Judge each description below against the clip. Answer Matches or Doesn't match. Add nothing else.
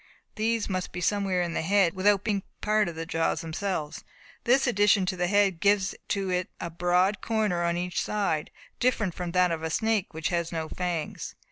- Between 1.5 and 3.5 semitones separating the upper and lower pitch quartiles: Matches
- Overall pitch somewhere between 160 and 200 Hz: Matches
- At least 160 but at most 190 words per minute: Doesn't match